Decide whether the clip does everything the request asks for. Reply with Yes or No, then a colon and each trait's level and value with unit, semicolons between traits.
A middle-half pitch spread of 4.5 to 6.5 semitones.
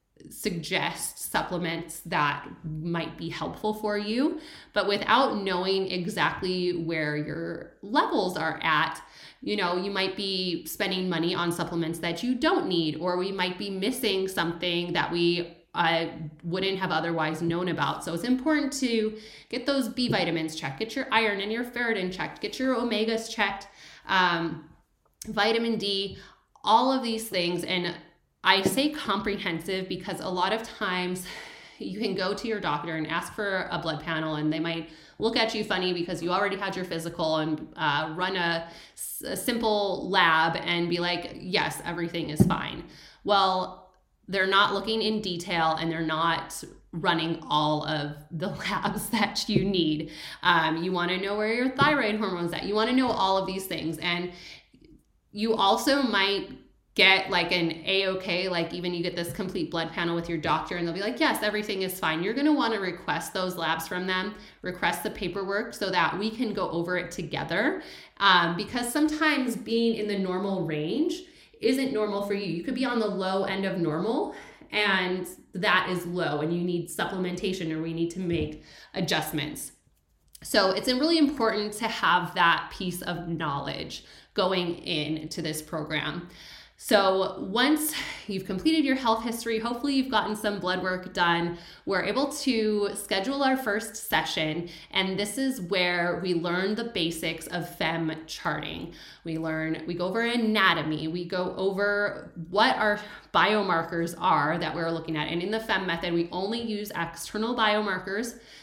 No: average, 3.9 semitones